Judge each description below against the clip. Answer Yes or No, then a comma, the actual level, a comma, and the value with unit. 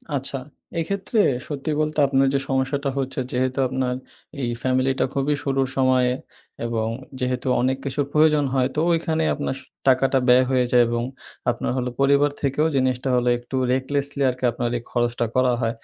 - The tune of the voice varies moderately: No, narrow, 1.9 semitones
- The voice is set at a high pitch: No, low, 130 Hz